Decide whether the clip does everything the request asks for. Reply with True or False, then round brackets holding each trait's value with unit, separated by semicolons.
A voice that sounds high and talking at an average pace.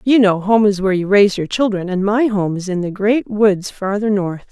False (200 Hz; 255 wpm)